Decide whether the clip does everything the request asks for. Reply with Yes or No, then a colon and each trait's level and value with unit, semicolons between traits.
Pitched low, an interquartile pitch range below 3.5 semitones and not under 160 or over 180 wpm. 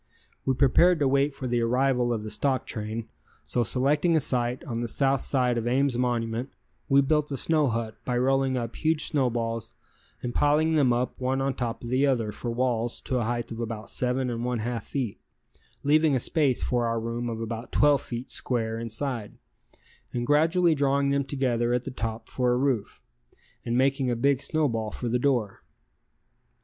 No: low, 125 Hz; average, 2.8 semitones; average, 190 wpm